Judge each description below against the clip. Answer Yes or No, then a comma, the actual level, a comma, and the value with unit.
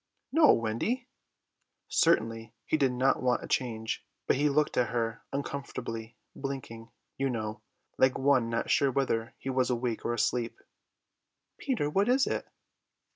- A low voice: Yes, low, 125 Hz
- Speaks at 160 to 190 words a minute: No, average, 145 wpm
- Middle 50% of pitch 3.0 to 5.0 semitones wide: Yes, average, 3.5 semitones